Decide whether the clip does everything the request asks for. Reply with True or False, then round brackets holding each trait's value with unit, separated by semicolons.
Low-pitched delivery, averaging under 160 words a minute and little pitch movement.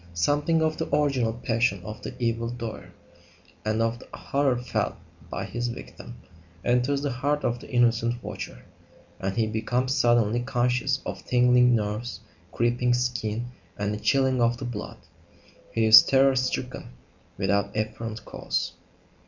True (120 Hz; 145 wpm; 2.0 semitones)